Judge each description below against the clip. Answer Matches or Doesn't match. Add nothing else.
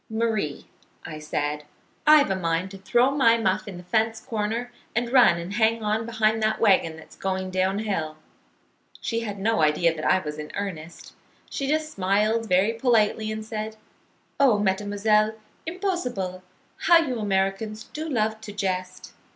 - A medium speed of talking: Matches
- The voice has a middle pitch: Doesn't match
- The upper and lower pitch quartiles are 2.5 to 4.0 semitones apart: Matches